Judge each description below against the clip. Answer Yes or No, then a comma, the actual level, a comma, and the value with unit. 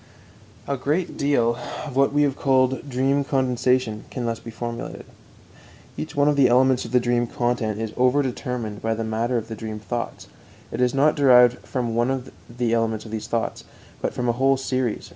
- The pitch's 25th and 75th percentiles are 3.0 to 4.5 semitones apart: No, narrow, 2.5 semitones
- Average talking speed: Yes, average, 185 wpm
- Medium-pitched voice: No, low, 125 Hz